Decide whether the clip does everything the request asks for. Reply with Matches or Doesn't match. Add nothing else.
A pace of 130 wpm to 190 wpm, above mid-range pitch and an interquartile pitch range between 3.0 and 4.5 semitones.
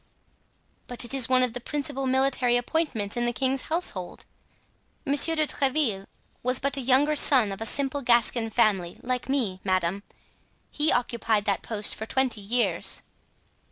Matches